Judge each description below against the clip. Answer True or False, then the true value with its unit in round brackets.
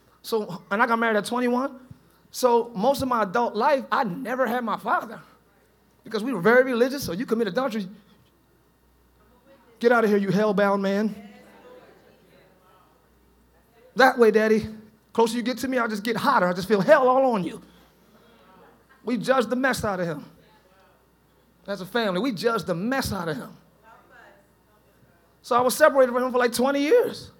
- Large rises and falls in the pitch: False (3.3 semitones)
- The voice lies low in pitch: False (235 Hz)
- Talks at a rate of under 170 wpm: False (175 wpm)